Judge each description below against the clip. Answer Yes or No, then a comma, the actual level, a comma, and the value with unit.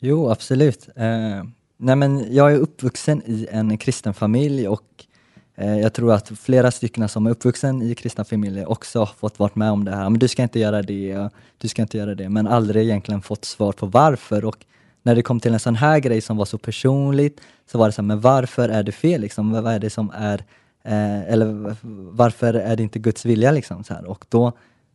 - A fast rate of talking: Yes, fast, 225 wpm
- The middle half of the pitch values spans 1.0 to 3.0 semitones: Yes, average, 2.7 semitones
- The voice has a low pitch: Yes, low, 115 Hz